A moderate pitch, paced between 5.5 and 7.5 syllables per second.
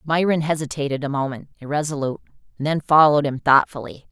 Yes: medium, 145 Hz; 6.5 syllables/s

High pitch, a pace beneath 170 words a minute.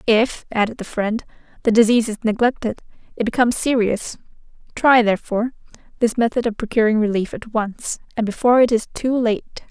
Yes: high, 225 Hz; average, 160 wpm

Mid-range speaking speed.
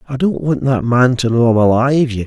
No: fast, 240 wpm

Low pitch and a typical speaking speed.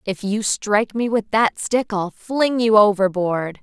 No: high, 210 Hz; average, 180 wpm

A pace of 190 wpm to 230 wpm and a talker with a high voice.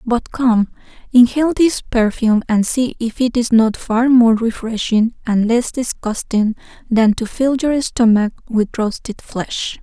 No: average, 155 wpm; high, 235 Hz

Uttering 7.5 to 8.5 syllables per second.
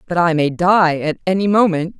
No: 5.1 syllables/s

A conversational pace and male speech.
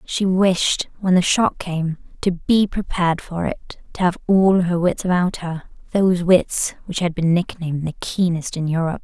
No: average, 180 wpm; female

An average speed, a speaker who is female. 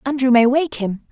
No: fast, 215 wpm; female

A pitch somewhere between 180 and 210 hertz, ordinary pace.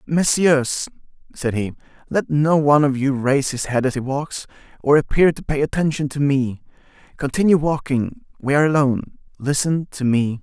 No: medium, 140 Hz; average, 165 wpm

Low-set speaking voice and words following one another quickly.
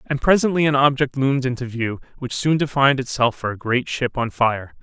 Yes: low, 130 Hz; fast, 210 wpm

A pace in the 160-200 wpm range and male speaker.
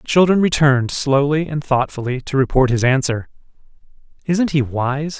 No: average, 150 wpm; male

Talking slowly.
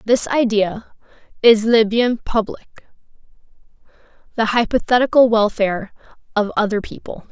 Yes: slow, 100 wpm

